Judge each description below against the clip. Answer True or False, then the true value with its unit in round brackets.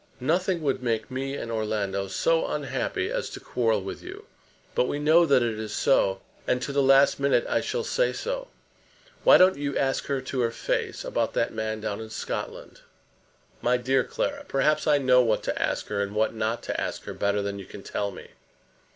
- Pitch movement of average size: True (4.7 semitones)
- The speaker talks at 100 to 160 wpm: False (205 wpm)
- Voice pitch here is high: False (125 Hz)